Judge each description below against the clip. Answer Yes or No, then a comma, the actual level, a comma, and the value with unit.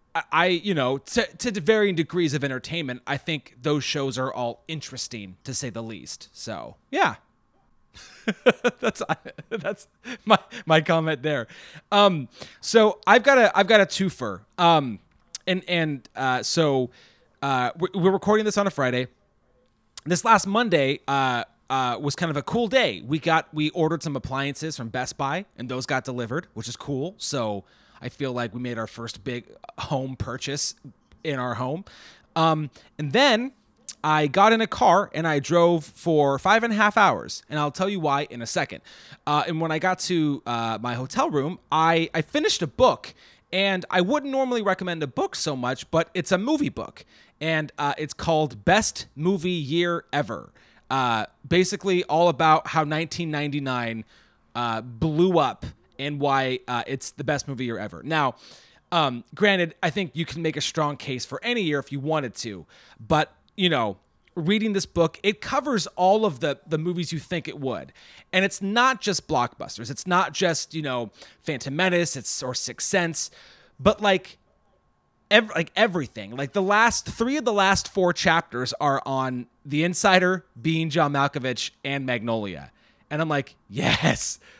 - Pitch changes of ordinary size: No, wide, 5.8 semitones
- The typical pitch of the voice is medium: Yes, medium, 155 Hz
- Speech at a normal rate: Yes, average, 175 wpm